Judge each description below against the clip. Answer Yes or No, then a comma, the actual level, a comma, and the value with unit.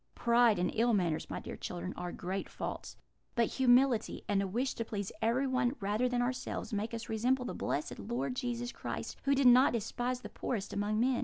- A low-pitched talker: No, high, 235 Hz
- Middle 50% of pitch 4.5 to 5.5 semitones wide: No, average, 3.4 semitones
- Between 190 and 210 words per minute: Yes, average, 200 wpm